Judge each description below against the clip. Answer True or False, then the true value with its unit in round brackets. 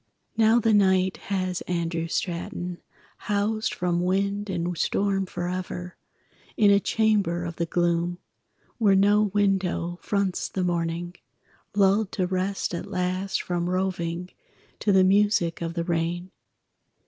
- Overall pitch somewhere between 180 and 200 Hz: True (185 Hz)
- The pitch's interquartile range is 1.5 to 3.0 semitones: True (2.4 semitones)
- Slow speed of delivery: True (130 wpm)